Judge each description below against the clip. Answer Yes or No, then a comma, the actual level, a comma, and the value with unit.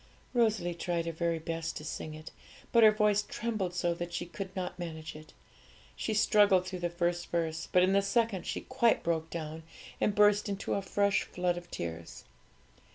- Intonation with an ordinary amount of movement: Yes, average, 3.5 semitones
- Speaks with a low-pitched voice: No, medium, 175 Hz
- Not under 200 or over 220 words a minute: No, average, 190 wpm